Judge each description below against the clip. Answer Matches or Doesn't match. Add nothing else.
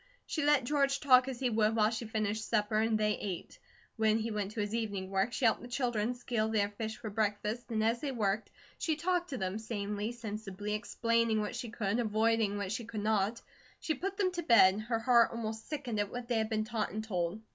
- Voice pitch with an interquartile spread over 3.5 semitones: Doesn't match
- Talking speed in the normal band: Doesn't match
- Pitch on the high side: Matches